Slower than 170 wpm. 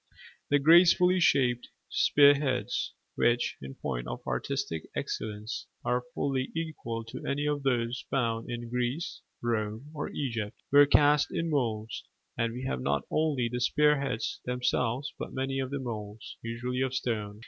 Yes: average, 155 wpm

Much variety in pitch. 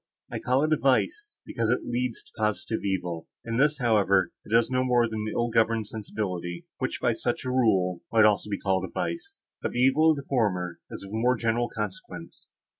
No: average, 4.1 semitones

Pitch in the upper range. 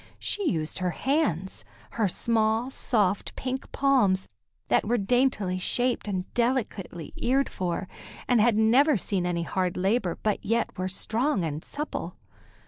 Yes: high, 215 Hz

